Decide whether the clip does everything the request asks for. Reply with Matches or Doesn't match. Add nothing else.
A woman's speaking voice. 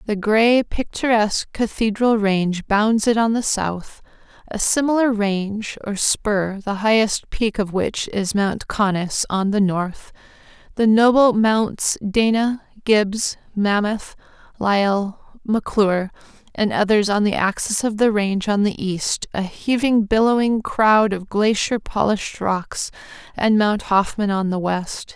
Matches